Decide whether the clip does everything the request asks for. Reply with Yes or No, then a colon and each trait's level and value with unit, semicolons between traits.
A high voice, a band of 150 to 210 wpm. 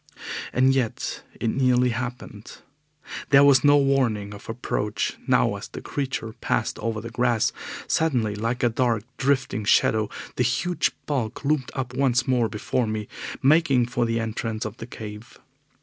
No: low, 120 Hz; average, 155 wpm